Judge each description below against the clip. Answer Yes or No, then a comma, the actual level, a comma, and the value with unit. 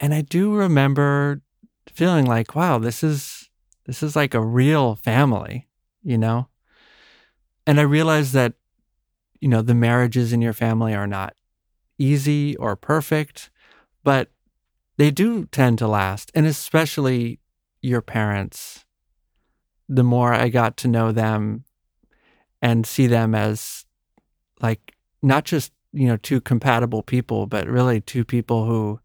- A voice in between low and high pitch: No, low, 125 Hz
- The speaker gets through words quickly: No, average, 140 wpm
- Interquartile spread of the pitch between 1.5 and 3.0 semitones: No, average, 4.3 semitones